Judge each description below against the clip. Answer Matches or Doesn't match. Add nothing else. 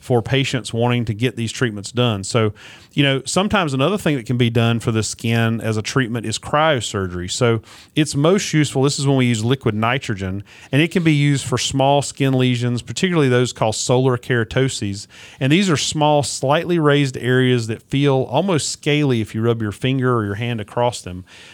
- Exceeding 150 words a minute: Matches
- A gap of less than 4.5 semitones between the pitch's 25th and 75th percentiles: Matches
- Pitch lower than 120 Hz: Doesn't match